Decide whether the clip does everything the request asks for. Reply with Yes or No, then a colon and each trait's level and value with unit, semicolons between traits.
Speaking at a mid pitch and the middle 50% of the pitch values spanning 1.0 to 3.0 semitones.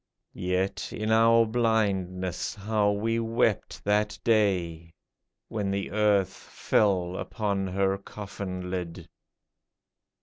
No: low, 100 Hz; average, 2.7 semitones